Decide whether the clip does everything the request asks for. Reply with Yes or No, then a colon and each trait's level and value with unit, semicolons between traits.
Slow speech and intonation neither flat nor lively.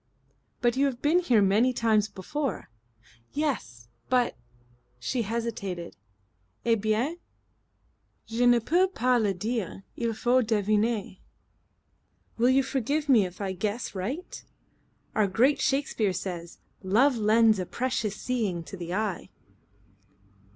Yes: slow, 125 wpm; average, 4.4 semitones